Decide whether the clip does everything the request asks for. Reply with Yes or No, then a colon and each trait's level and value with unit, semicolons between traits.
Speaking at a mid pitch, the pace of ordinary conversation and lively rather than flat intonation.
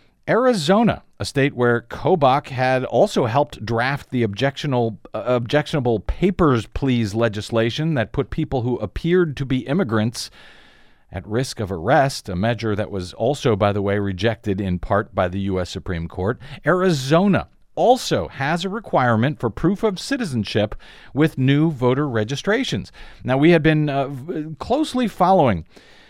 No: low, 130 Hz; average, 145 wpm; wide, 6.3 semitones